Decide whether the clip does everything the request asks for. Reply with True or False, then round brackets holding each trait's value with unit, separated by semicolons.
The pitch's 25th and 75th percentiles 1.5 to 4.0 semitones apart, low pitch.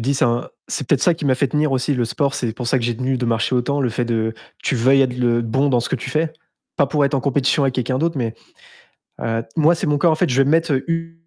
True (3.3 semitones; 130 Hz)